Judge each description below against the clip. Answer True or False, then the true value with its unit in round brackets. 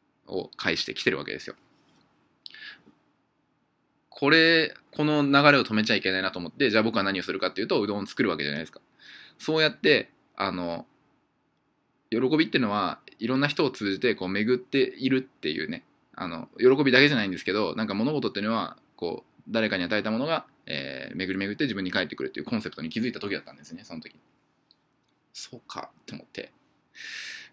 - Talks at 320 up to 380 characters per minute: False (395 characters per minute)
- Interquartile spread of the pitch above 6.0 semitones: True (6.8 semitones)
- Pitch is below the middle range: True (125 Hz)